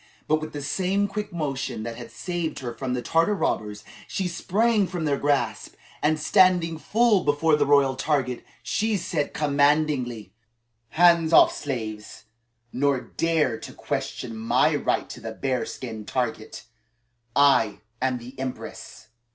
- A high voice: No, medium, 145 Hz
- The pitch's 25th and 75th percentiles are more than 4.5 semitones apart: Yes, average, 5.0 semitones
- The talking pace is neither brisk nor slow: Yes, average, 145 wpm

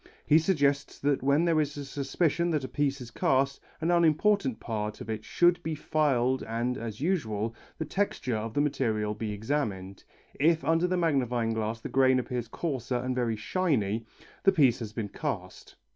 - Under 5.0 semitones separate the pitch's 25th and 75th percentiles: No, wide, 5.5 semitones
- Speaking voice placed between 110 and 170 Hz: Yes, low, 135 Hz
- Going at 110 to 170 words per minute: No, average, 180 wpm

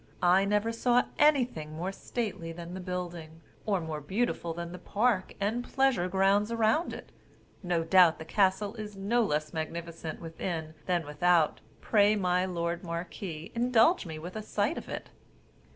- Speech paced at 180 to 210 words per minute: No, average, 160 wpm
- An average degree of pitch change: Yes, average, 4.1 semitones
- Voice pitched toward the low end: No, medium, 185 Hz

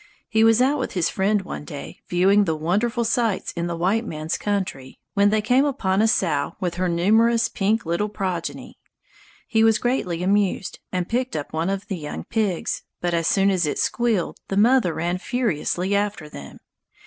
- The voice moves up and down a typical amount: Yes, average, 4.4 semitones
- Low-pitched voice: No, high, 195 Hz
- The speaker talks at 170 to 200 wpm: Yes, average, 185 wpm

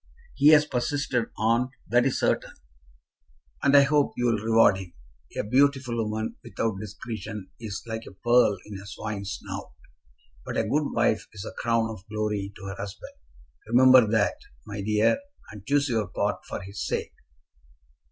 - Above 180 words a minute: No, average, 160 wpm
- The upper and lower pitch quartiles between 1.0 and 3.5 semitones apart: Yes, average, 3.2 semitones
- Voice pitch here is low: Yes, low, 110 Hz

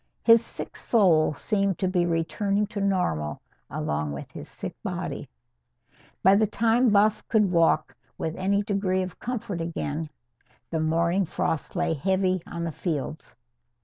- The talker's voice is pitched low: No, medium, 185 Hz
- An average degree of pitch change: Yes, average, 3.7 semitones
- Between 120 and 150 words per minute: Yes, average, 145 wpm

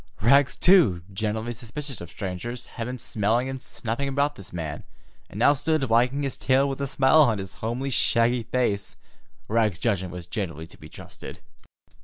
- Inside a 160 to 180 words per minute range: Yes, average, 175 wpm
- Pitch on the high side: No, low, 115 Hz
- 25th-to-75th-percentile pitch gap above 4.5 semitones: Yes, average, 5.1 semitones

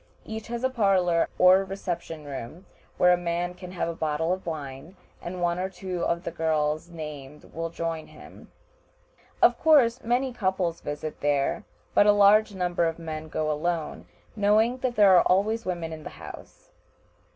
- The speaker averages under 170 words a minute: No, average, 175 wpm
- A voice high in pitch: No, medium, 175 Hz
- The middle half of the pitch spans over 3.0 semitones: Yes, average, 3.7 semitones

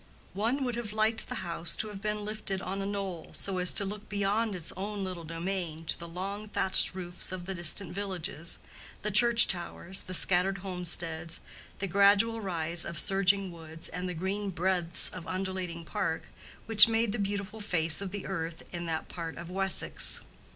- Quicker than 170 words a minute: Yes, average, 185 wpm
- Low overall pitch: No, high, 190 Hz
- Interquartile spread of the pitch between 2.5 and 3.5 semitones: Yes, average, 2.9 semitones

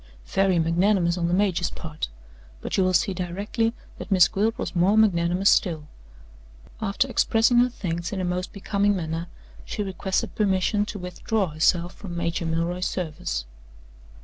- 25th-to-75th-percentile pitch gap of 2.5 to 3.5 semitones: Yes, average, 3.0 semitones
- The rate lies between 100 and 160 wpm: Yes, average, 155 wpm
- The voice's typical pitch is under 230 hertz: Yes, medium, 185 Hz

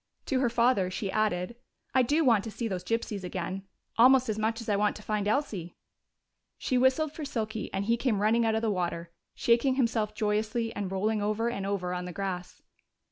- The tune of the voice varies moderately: Yes, average, 3.2 semitones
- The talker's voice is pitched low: No, high, 215 Hz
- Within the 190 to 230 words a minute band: Yes, fast, 205 wpm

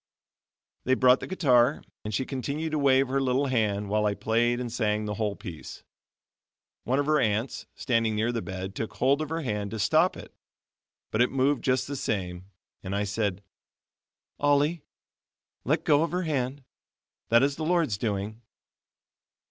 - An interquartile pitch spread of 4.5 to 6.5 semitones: Yes, average, 5.0 semitones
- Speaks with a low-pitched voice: Yes, low, 120 Hz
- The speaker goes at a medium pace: Yes, average, 170 wpm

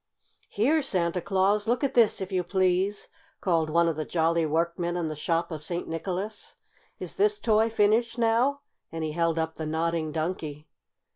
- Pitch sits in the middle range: Yes, medium, 175 Hz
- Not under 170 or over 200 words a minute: Yes, average, 175 wpm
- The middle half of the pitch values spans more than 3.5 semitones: Yes, average, 4.5 semitones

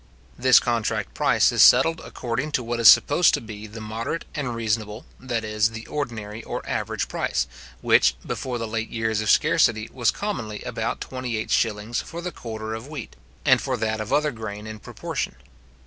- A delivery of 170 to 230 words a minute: Yes, average, 180 wpm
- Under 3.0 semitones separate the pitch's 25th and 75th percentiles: Yes, narrow, 2.6 semitones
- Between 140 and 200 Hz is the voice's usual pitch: No, low, 115 Hz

